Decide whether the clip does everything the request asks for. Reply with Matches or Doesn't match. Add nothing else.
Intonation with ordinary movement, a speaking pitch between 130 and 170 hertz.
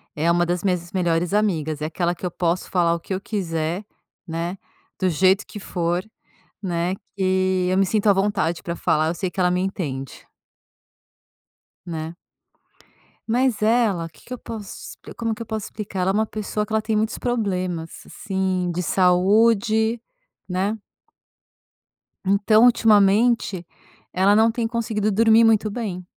Doesn't match